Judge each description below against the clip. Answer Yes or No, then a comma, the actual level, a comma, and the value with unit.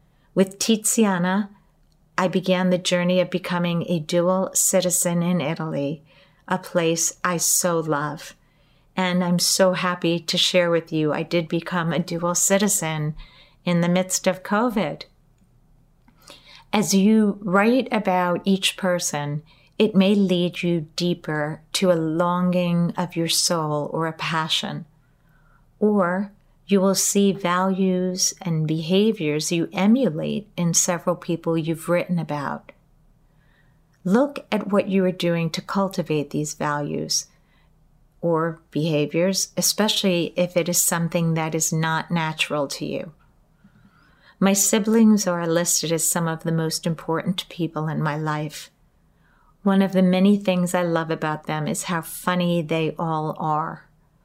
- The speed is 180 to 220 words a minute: No, slow, 135 wpm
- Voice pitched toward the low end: No, medium, 175 Hz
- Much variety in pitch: No, average, 2.7 semitones